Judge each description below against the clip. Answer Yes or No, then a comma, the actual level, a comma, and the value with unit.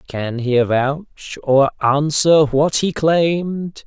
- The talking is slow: Yes, slow, 125 wpm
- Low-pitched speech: No, medium, 145 Hz